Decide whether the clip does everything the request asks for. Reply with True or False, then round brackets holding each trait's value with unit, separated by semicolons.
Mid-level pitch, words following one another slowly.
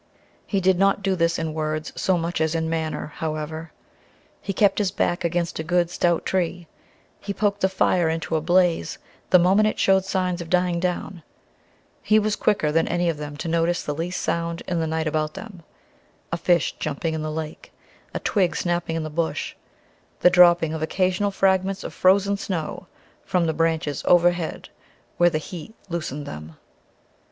False (170 Hz; 180 wpm)